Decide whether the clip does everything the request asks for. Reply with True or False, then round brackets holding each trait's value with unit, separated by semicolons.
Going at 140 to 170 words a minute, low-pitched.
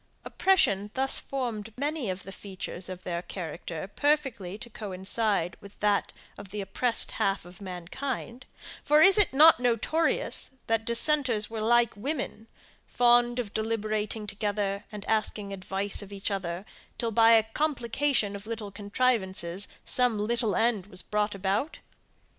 False (145 wpm; 215 Hz)